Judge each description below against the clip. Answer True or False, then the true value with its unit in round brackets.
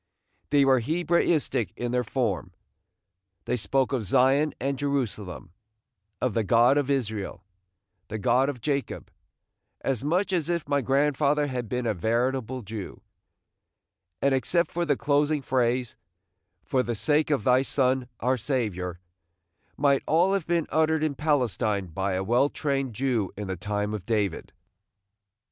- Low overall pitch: True (130 Hz)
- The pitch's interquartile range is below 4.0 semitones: False (4.5 semitones)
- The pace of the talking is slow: False (150 wpm)